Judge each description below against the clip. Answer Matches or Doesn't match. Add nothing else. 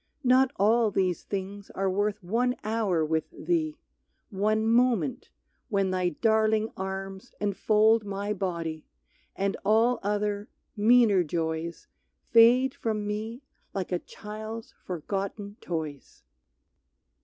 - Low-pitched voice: Doesn't match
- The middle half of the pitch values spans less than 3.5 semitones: Matches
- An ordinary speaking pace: Doesn't match